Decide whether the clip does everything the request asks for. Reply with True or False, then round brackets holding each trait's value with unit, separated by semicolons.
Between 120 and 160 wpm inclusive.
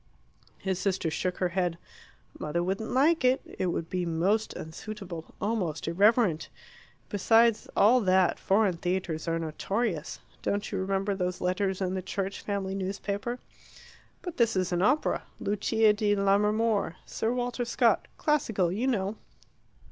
True (140 wpm)